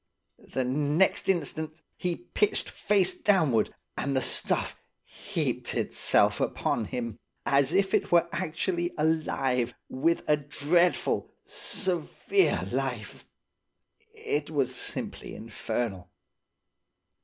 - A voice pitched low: No, medium, 155 Hz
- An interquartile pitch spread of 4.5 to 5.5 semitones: Yes, average, 5.2 semitones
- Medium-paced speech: No, slow, 100 wpm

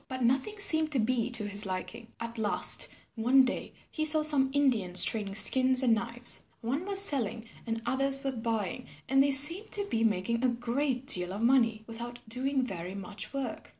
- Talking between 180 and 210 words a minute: Yes, average, 185 wpm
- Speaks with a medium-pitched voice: No, high, 245 Hz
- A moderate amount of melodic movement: Yes, average, 3.4 semitones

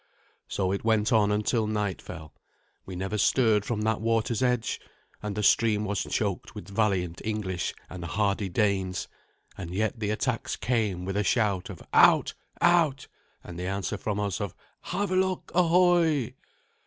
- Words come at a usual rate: Yes, average, 155 wpm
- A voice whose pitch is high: No, low, 105 Hz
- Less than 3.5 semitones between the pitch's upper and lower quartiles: Yes, average, 3.0 semitones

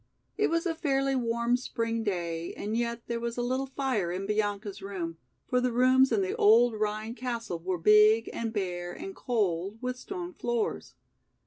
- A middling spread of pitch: Yes, average, 3.9 semitones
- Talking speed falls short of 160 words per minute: No, average, 180 wpm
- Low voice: No, high, 230 Hz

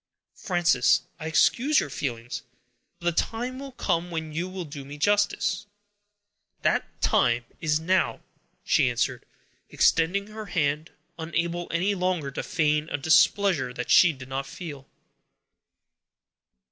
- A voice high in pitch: No, medium, 165 Hz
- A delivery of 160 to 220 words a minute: No, slow, 135 wpm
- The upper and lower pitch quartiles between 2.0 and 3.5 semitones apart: No, average, 4.5 semitones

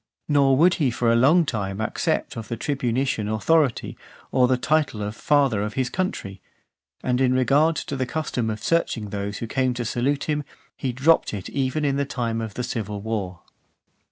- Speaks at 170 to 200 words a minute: Yes, average, 190 wpm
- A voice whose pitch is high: No, low, 125 Hz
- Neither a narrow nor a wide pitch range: Yes, average, 4.3 semitones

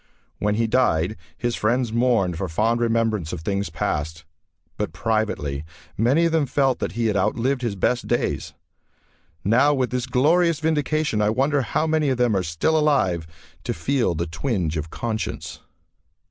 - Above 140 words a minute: Yes, average, 165 wpm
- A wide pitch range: Yes, wide, 6.1 semitones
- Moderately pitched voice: No, low, 115 Hz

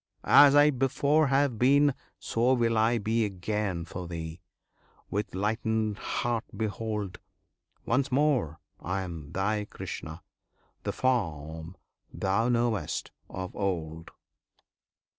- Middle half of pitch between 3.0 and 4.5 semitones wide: No, average, 5.2 semitones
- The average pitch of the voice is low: Yes, low, 110 Hz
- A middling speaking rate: No, slow, 110 wpm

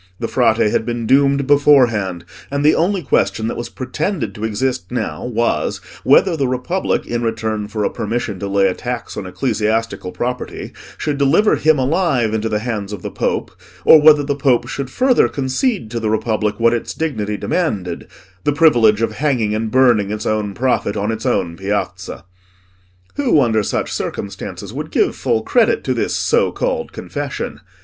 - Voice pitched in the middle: No, low, 115 Hz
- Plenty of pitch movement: No, average, 4.8 semitones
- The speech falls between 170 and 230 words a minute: Yes, average, 175 wpm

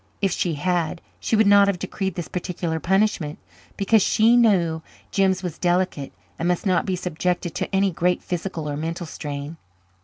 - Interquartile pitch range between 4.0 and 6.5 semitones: No, average, 2.8 semitones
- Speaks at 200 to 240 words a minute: No, average, 175 wpm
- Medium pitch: Yes, medium, 180 Hz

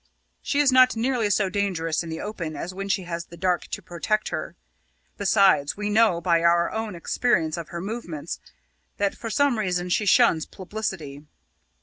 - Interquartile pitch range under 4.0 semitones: No, average, 4.3 semitones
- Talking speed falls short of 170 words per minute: No, average, 180 wpm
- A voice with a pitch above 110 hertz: Yes, high, 190 Hz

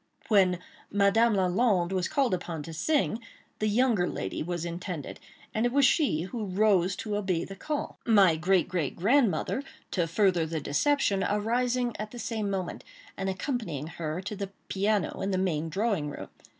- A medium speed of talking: Yes, average, 170 wpm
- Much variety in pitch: No, average, 4.3 semitones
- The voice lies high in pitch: Yes, high, 195 Hz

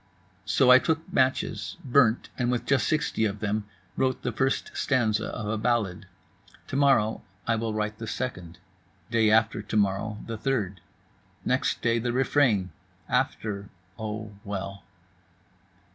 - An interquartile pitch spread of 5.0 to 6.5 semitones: No, average, 3.4 semitones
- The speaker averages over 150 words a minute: No, average, 140 wpm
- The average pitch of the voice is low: Yes, low, 110 Hz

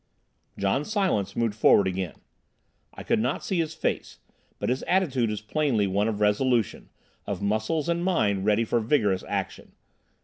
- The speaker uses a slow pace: No, average, 160 wpm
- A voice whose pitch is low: Yes, low, 110 Hz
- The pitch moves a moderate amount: No, wide, 6.5 semitones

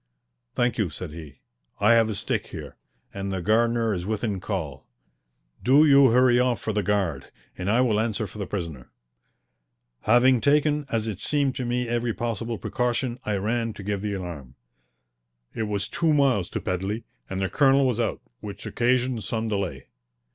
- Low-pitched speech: Yes, low, 110 Hz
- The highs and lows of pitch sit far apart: No, average, 3.9 semitones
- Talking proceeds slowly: No, average, 175 wpm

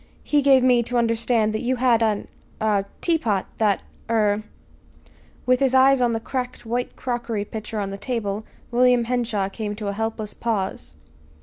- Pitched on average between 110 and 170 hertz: No, high, 225 Hz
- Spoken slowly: No, average, 170 wpm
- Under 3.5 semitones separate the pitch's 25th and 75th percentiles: Yes, average, 3.1 semitones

